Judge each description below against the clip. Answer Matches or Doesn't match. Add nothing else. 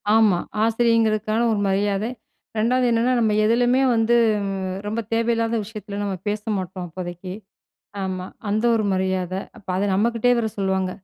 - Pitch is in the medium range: Doesn't match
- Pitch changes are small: Doesn't match